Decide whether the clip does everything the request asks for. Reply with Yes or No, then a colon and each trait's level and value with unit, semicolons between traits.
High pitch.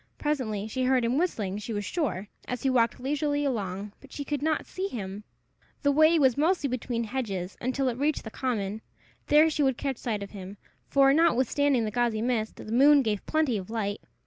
Yes: very high, 250 Hz